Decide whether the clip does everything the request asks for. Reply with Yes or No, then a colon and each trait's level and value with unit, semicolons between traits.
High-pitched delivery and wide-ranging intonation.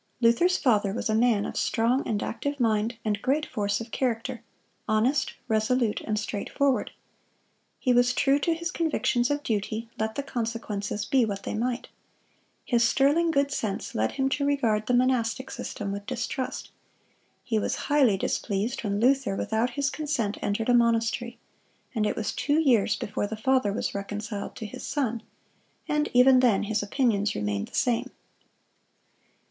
No: high, 235 Hz; average, 3.9 semitones